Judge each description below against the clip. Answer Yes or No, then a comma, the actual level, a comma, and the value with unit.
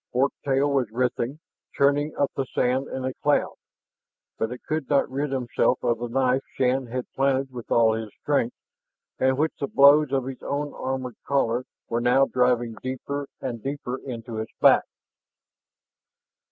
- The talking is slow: No, average, 165 wpm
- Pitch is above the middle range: No, low, 130 Hz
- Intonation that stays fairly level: Yes, narrow, 2.1 semitones